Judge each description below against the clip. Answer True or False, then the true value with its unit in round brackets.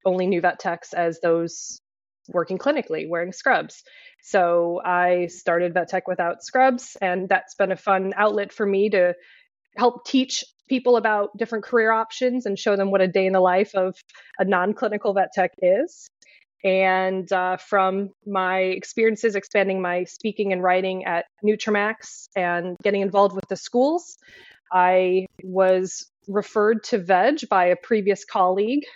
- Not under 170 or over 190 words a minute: False (155 wpm)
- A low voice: False (195 Hz)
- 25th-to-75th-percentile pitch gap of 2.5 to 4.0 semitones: True (3.4 semitones)